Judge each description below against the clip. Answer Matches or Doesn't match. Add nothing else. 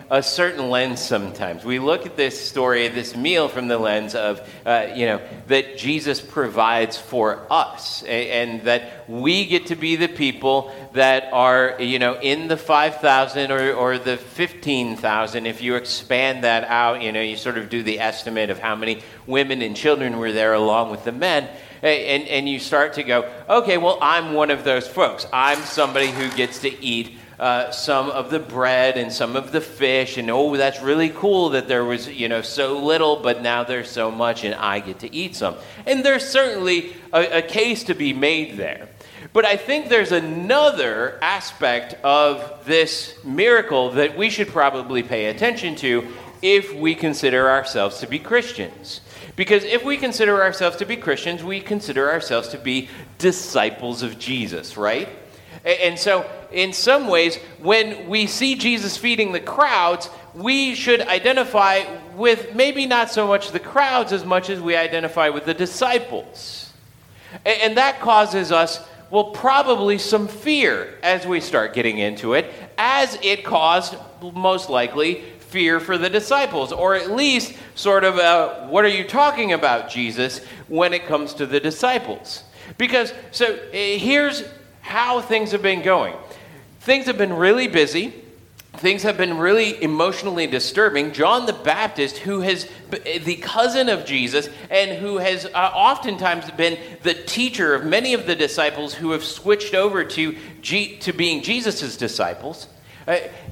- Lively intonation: Matches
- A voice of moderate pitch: Matches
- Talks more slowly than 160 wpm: Doesn't match